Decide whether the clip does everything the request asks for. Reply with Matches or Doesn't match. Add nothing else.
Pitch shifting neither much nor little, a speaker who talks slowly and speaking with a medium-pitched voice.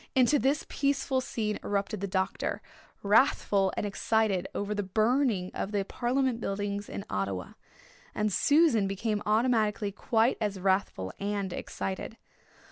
Doesn't match